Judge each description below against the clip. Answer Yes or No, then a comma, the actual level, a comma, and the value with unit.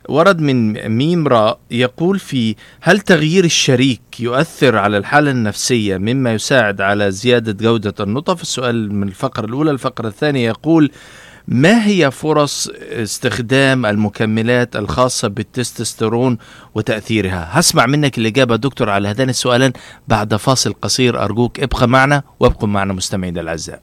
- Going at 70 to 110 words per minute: No, average, 130 wpm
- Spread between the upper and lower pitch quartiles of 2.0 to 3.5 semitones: No, average, 4.1 semitones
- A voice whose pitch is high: No, low, 125 Hz